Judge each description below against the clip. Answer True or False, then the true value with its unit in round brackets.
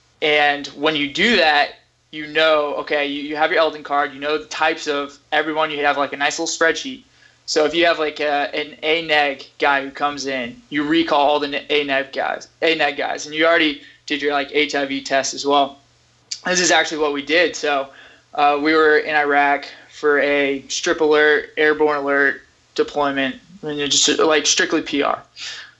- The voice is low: False (150 Hz)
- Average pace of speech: True (190 wpm)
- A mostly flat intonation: True (1.5 semitones)